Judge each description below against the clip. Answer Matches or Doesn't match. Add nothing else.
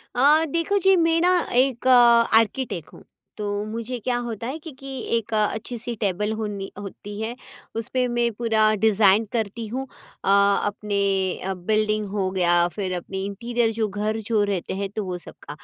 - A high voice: Matches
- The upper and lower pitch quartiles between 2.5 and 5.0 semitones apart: Matches